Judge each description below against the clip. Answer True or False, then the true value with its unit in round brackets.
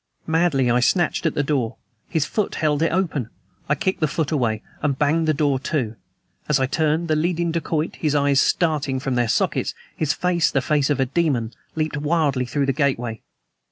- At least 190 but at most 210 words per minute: True (195 wpm)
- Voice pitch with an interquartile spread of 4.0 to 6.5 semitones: False (3.2 semitones)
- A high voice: False (150 Hz)